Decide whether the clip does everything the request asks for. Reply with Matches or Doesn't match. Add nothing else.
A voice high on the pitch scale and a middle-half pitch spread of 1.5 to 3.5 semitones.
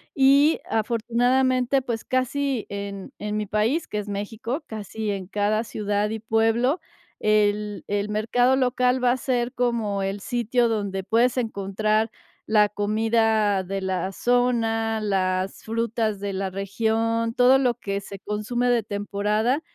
Matches